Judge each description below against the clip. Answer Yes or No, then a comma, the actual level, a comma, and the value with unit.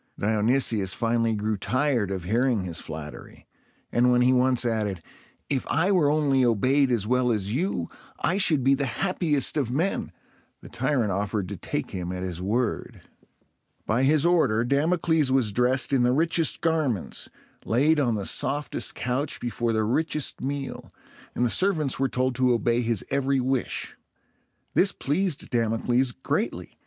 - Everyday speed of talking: Yes, average, 160 wpm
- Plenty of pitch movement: No, average, 4.3 semitones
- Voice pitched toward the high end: No, low, 125 Hz